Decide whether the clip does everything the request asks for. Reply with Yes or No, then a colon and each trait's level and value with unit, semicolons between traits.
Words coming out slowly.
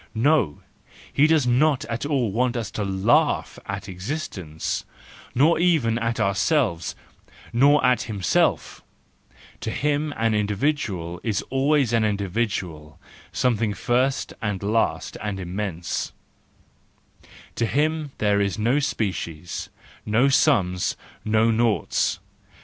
Yes: slow, 115 wpm